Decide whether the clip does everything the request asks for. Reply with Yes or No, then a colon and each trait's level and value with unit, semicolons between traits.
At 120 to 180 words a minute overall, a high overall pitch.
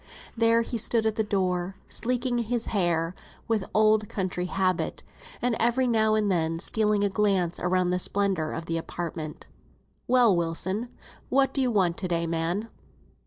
Yes: average, 170 wpm; high, 200 Hz